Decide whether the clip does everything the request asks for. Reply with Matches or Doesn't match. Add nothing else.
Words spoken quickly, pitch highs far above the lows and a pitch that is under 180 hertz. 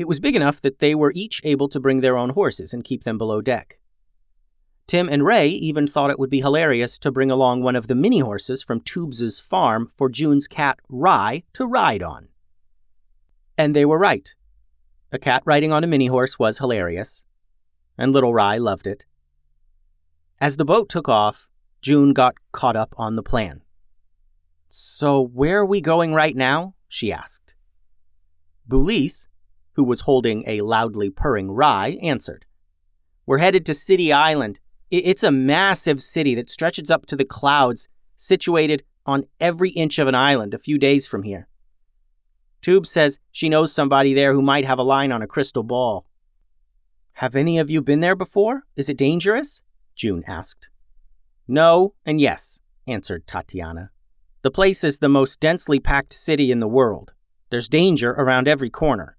Doesn't match